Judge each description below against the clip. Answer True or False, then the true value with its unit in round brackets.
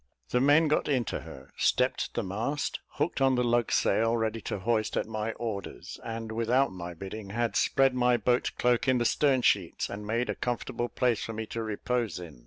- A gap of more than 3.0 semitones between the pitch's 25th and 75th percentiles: False (2.4 semitones)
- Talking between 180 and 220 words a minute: True (200 wpm)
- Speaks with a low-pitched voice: True (115 Hz)